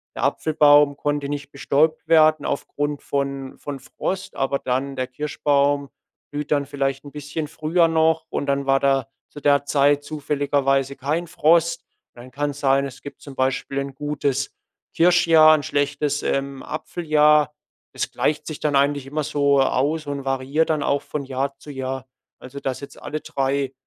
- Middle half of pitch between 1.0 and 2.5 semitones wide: Yes, narrow, 1.6 semitones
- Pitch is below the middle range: No, medium, 145 Hz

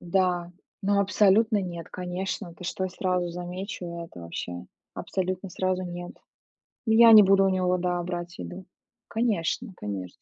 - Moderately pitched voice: Yes, medium, 180 Hz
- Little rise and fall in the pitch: Yes, narrow, 1.8 semitones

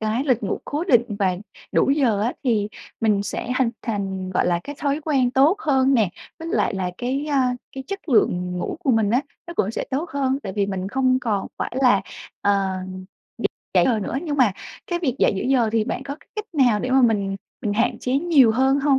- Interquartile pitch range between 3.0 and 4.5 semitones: No, average, 5.1 semitones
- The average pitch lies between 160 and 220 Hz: No, very high, 250 Hz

